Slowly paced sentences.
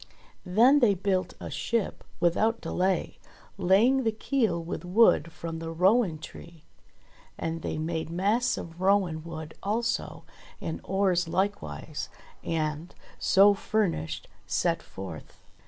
Yes: slow, 120 wpm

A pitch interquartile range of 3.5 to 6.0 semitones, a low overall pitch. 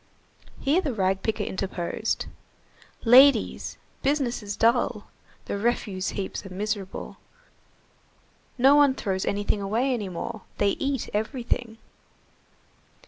No: average, 4.1 semitones; high, 220 Hz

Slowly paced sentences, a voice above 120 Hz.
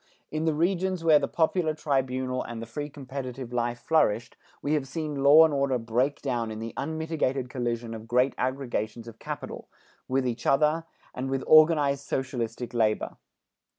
No: average, 165 wpm; low, 135 Hz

